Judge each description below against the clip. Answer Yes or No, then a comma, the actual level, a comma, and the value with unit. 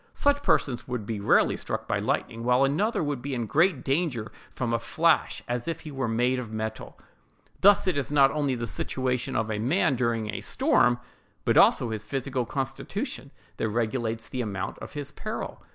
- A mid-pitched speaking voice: No, low, 125 Hz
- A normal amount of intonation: Yes, average, 3.8 semitones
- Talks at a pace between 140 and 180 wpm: No, average, 195 wpm